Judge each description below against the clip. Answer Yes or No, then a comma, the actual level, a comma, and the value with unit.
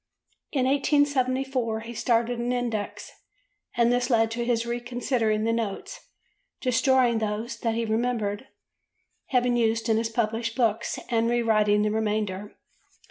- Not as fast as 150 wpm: Yes, slow, 135 wpm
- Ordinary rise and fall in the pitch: No, narrow, 1.8 semitones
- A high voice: Yes, high, 230 Hz